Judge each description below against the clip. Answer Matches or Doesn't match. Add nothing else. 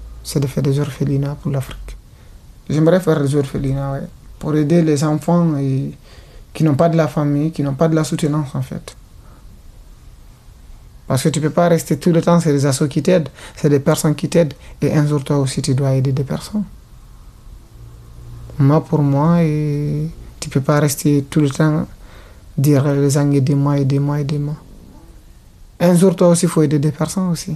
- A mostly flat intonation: Matches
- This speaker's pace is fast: Doesn't match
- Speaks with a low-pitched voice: Doesn't match